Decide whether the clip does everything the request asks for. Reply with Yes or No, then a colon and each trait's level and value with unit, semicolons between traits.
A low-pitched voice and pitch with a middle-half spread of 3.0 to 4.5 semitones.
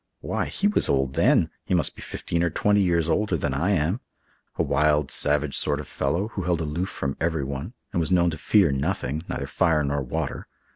Yes: very low, 80 Hz; average, 4.0 semitones